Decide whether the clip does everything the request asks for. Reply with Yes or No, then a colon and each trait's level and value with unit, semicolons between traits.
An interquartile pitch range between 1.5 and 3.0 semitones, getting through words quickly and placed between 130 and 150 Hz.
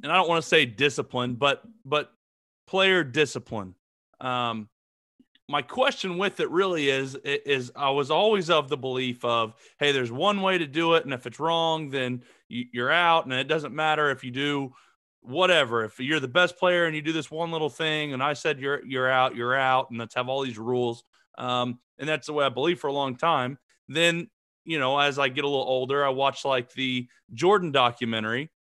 No: average, 4.3 semitones; fast, 210 wpm; medium, 140 Hz